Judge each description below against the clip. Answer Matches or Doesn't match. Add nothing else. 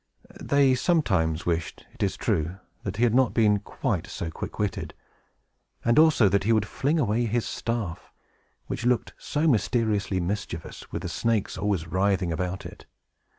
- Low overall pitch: Matches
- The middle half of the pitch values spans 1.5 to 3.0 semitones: Doesn't match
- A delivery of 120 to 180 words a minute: Matches